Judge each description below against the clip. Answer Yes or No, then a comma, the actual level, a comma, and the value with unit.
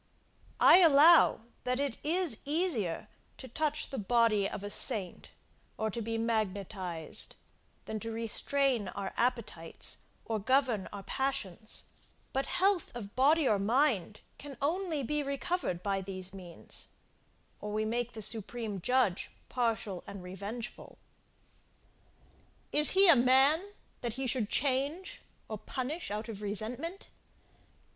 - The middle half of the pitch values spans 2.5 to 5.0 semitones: No, wide, 5.4 semitones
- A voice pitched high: Yes, high, 235 Hz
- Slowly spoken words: Yes, slow, 130 wpm